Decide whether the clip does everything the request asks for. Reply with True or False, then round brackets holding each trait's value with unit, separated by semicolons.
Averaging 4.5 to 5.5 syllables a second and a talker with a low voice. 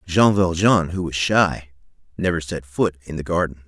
True (4.6 syllables/s; 85 Hz)